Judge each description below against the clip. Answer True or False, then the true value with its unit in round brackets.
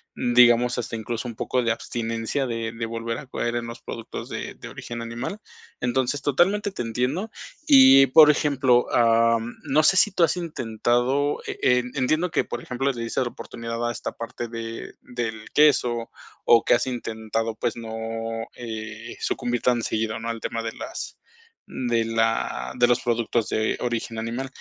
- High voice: False (120 Hz)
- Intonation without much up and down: True (2.2 semitones)